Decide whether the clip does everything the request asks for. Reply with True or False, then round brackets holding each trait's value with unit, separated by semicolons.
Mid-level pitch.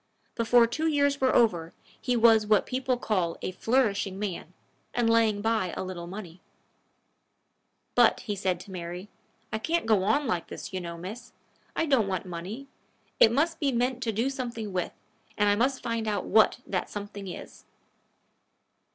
False (220 Hz)